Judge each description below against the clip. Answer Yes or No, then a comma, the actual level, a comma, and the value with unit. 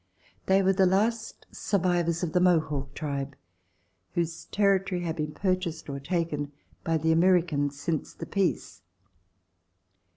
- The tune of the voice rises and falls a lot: No, average, 3.6 semitones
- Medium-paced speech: No, slow, 130 wpm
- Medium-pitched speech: Yes, medium, 170 Hz